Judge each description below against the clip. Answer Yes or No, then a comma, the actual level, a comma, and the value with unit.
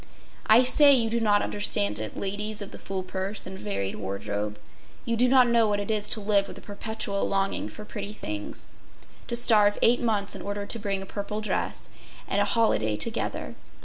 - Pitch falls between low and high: No, high, 205 Hz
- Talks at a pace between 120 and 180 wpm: No, average, 195 wpm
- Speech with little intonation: Yes, narrow, 2.2 semitones